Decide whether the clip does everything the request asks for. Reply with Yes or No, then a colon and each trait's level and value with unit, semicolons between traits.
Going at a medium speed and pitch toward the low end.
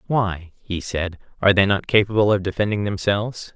Yes: average, 170 wpm; low, 100 Hz